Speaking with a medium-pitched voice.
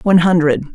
Yes: medium, 170 Hz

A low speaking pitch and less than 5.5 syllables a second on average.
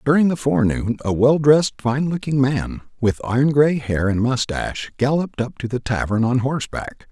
Yes: low, 130 Hz; 5.3 syllables/s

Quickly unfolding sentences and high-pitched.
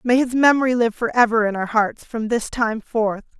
Yes: fast, 230 wpm; high, 230 Hz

